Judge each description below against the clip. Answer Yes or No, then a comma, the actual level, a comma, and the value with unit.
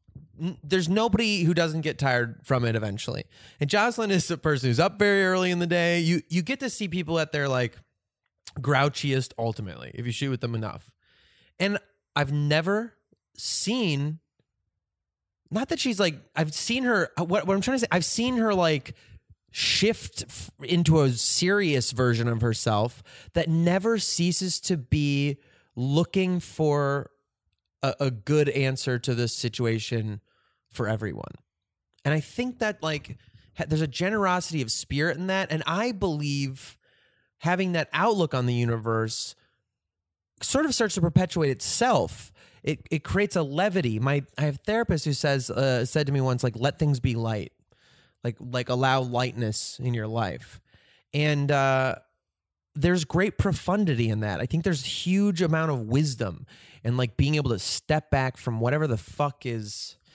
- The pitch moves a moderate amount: No, wide, 6.4 semitones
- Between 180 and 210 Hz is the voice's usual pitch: No, medium, 145 Hz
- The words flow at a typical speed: Yes, average, 165 wpm